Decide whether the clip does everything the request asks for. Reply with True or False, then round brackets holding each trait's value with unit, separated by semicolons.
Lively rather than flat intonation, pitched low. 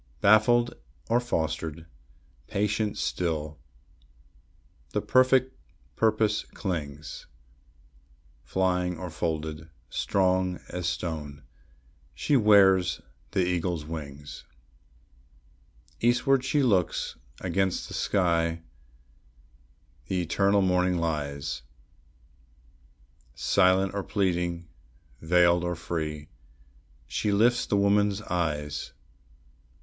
False (3.9 semitones; 90 Hz)